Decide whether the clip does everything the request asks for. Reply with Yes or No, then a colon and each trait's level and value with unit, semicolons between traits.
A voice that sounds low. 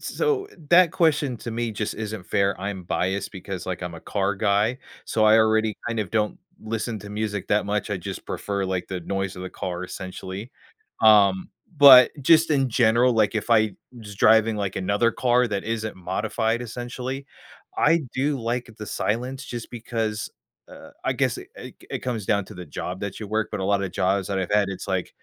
Yes: low, 110 Hz